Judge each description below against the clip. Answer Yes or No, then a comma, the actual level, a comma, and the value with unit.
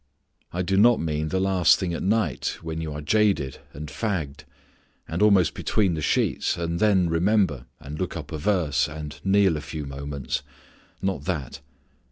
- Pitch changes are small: No, average, 4.4 semitones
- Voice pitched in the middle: No, very low, 85 Hz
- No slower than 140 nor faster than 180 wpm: Yes, average, 175 wpm